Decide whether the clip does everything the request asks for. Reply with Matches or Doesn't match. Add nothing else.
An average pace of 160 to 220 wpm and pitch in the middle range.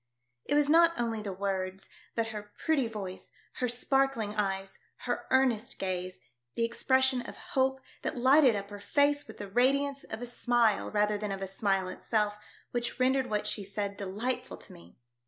Doesn't match